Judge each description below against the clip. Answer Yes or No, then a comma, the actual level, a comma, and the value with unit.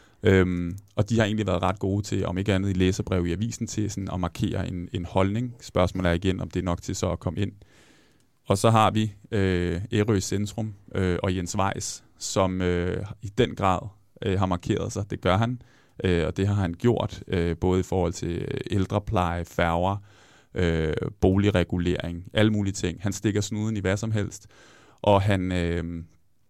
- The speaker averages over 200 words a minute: No, average, 190 wpm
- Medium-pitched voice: No, very low, 95 Hz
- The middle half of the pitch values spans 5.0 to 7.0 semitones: No, average, 2.9 semitones